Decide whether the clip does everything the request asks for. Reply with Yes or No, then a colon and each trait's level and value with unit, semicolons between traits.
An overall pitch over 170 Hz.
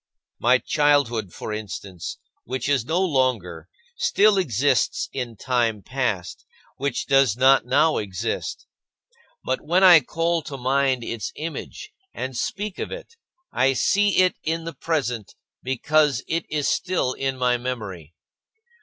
No: low, 130 Hz